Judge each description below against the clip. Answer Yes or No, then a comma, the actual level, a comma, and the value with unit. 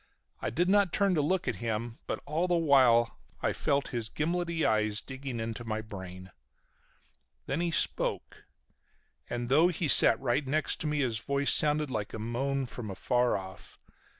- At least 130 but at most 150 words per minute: No, average, 175 wpm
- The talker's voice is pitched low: Yes, low, 130 Hz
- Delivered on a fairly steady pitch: No, wide, 5.4 semitones